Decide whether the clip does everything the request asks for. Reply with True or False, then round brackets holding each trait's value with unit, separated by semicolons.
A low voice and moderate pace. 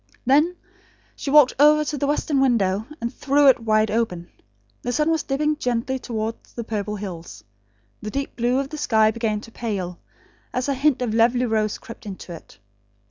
False (235 Hz; 185 wpm)